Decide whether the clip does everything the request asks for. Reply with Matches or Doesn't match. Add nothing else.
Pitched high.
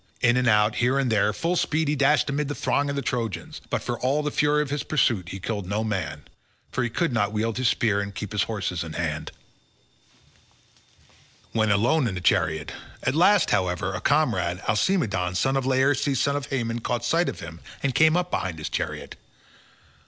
Doesn't match